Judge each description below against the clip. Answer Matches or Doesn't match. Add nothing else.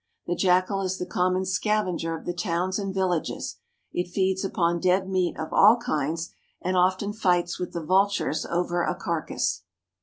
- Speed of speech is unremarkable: Matches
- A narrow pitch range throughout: Matches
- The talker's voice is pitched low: Doesn't match